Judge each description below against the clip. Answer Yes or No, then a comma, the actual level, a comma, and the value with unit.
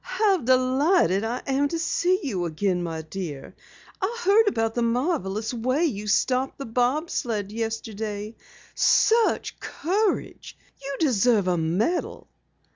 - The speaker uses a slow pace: Yes, slow, 130 wpm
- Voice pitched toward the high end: Yes, high, 245 Hz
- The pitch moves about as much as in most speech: No, wide, 7.3 semitones